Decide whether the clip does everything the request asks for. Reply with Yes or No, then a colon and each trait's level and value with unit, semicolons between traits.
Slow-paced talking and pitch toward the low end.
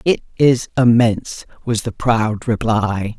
Yes: slow, 130 wpm; low, 115 Hz